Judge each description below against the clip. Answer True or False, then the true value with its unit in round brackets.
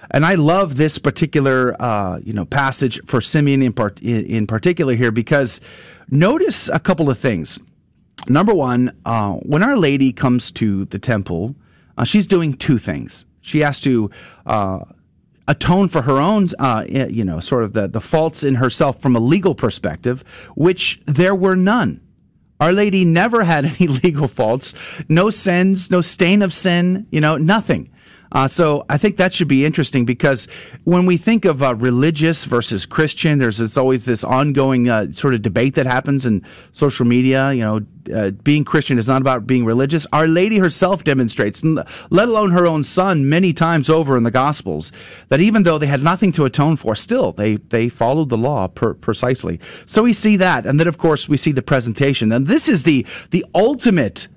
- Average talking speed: True (190 wpm)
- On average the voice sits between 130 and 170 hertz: True (140 Hz)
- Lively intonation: True (5.7 semitones)